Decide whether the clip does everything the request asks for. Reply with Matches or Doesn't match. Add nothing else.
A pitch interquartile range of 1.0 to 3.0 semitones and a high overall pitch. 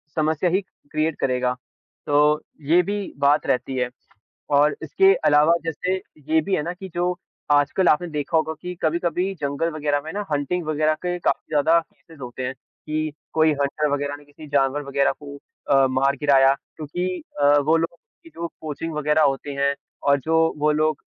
Doesn't match